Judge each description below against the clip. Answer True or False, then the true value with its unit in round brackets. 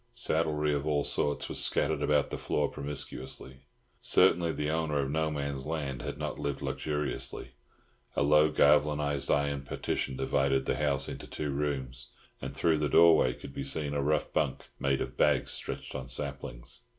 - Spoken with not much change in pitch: True (1.7 semitones)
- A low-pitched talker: True (75 Hz)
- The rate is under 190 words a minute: True (170 wpm)